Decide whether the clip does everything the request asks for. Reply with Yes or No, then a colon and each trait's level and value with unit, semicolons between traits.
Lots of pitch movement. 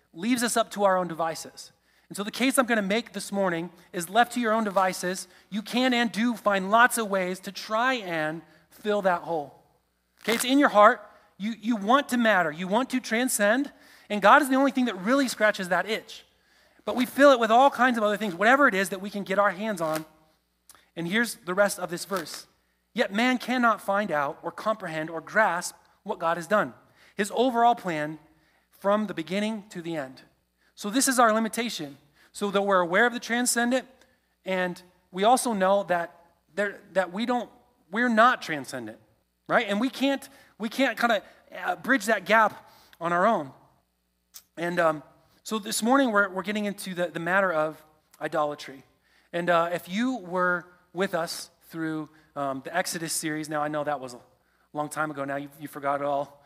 Yes: wide, 5.8 semitones